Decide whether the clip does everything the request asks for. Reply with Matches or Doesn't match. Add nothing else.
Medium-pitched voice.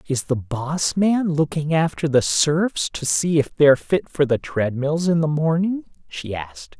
Matches